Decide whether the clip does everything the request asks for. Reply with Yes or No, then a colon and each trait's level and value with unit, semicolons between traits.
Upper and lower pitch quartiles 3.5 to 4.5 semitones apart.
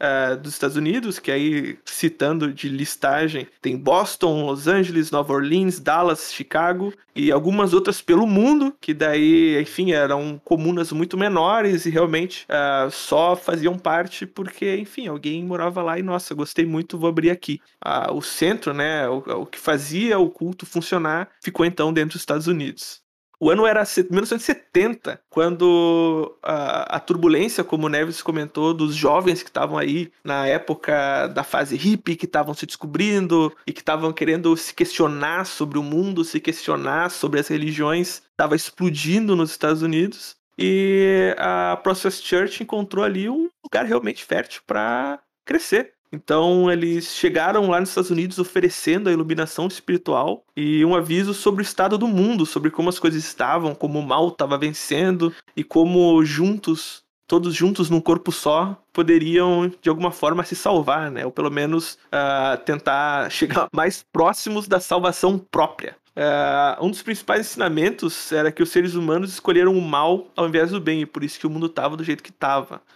No: average, 3.1 semitones